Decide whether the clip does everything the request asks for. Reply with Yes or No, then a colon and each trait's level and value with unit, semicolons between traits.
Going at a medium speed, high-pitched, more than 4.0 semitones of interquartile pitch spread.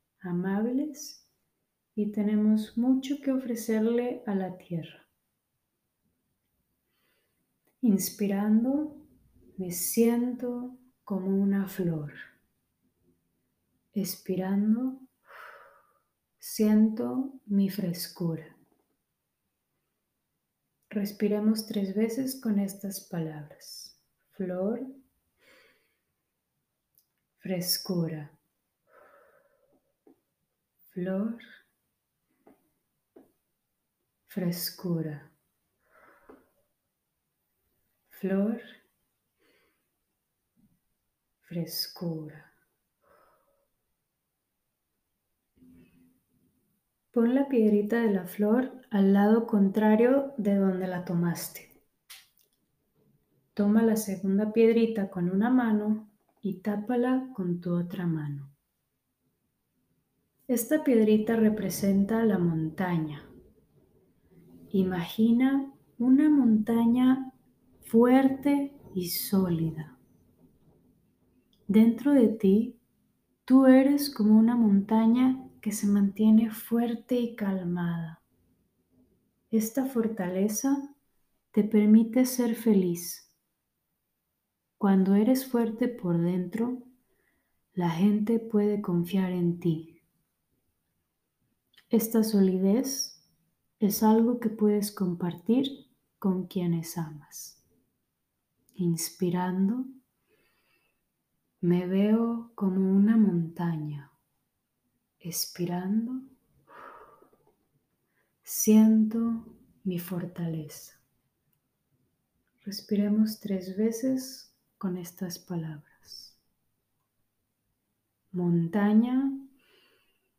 No: slow, 65 wpm; high, 205 Hz; average, 4.7 semitones